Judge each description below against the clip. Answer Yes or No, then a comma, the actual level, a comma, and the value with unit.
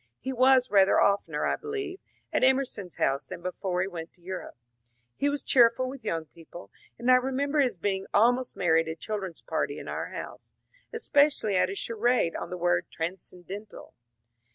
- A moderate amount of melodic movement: No, wide, 6.5 semitones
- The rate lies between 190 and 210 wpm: Yes, average, 195 wpm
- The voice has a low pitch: No, high, 200 Hz